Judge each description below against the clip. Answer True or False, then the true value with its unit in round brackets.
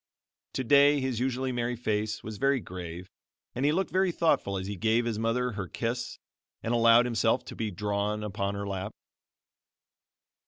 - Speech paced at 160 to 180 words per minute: True (165 wpm)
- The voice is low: True (115 Hz)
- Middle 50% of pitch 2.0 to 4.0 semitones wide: True (3.6 semitones)